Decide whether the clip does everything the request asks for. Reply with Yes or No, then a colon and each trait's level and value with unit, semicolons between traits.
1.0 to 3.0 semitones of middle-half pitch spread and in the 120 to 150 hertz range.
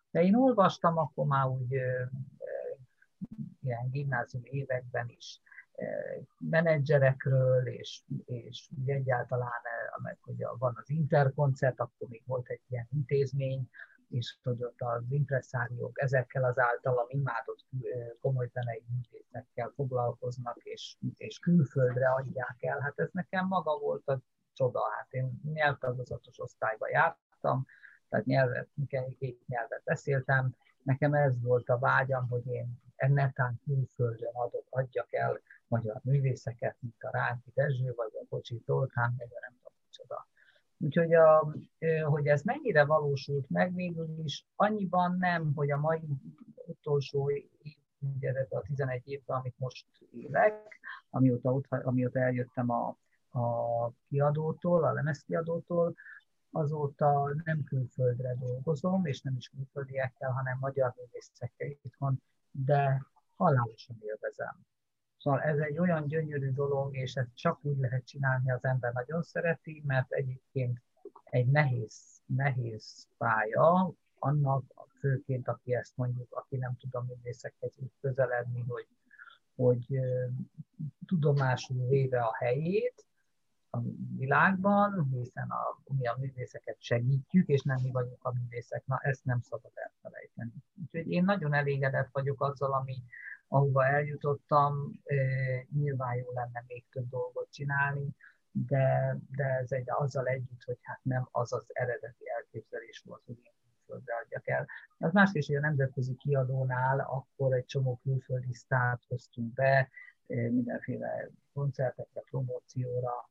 Yes: average, 2.7 semitones; low, 135 Hz